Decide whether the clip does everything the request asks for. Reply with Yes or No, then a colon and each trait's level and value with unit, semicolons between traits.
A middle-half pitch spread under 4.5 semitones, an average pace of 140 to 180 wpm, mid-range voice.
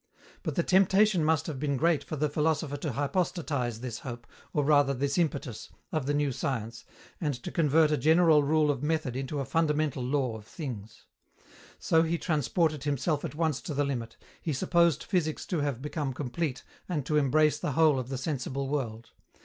No: average, 3.1 semitones; average, 190 wpm; medium, 145 Hz